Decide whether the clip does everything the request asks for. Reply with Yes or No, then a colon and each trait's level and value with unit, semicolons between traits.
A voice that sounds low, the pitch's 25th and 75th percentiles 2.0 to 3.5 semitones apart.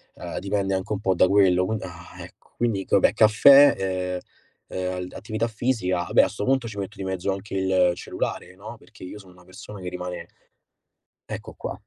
Yes: very low, 95 Hz; narrow, 2.5 semitones